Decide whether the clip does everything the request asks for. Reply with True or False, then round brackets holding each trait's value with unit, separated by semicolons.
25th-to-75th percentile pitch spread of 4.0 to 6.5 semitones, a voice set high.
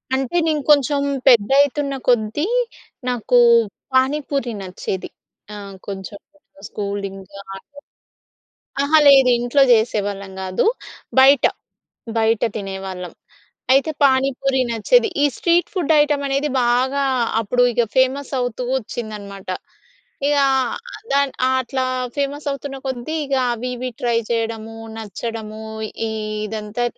True (4.6 semitones; 245 Hz)